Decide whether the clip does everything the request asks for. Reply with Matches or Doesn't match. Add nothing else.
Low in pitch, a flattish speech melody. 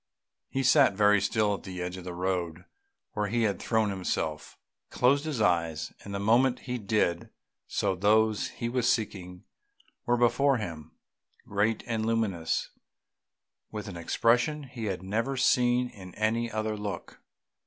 Doesn't match